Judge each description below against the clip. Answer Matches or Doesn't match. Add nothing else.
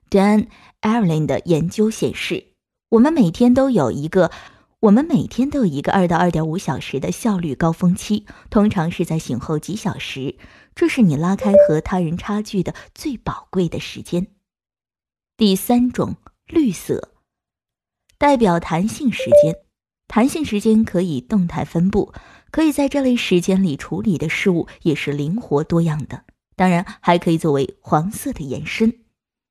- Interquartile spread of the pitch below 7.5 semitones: Matches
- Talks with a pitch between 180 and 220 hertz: Matches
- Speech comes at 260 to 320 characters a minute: Doesn't match